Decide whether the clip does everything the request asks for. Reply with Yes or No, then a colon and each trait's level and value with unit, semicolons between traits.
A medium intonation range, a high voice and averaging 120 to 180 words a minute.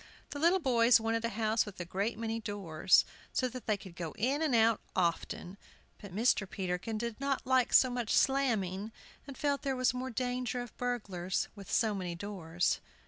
No: average, 4.6 semitones; high, 225 Hz; average, 190 wpm